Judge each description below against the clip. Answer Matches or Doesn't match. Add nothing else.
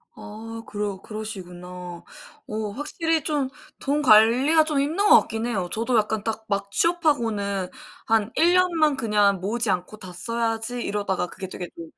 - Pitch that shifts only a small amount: Doesn't match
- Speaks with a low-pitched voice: Doesn't match